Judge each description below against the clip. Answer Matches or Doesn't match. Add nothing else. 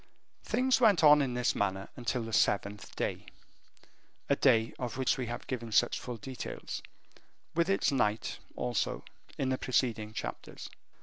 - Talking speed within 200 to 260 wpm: Doesn't match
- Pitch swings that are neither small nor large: Matches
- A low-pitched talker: Matches